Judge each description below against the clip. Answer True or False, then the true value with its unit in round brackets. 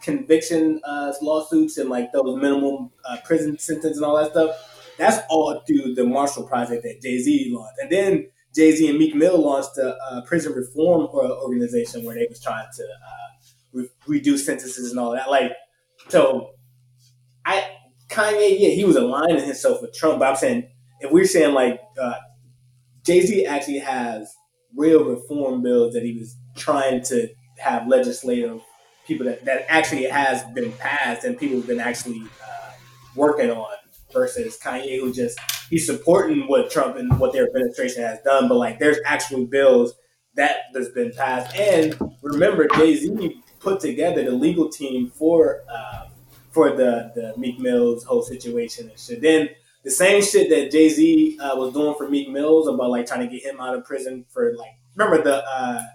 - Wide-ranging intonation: True (8.1 semitones)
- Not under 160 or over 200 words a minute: True (180 wpm)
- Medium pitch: True (150 Hz)